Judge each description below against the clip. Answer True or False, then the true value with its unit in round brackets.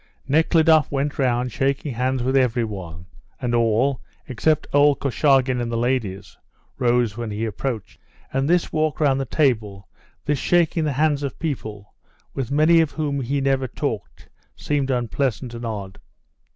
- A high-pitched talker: False (130 Hz)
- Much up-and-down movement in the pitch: False (3.6 semitones)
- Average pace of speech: True (155 wpm)